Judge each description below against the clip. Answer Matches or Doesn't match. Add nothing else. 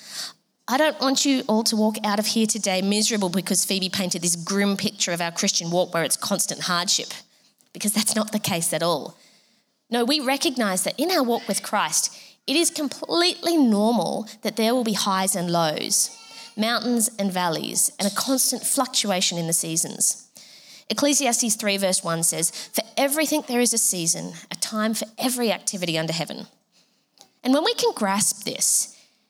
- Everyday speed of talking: Matches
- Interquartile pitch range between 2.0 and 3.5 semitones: Doesn't match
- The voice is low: Doesn't match